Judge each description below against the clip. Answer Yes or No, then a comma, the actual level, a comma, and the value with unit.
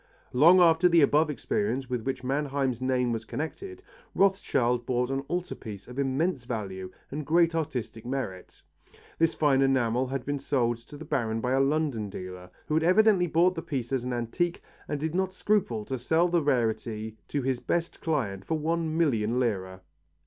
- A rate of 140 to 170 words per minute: No, average, 180 wpm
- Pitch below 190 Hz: Yes, low, 135 Hz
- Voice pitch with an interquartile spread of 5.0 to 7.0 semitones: Yes, average, 5.3 semitones